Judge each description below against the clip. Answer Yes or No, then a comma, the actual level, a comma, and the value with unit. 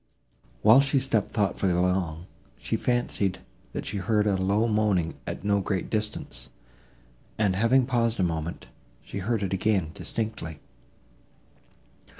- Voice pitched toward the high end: No, low, 100 Hz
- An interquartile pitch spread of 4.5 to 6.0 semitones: No, average, 3.3 semitones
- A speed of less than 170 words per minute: Yes, average, 140 wpm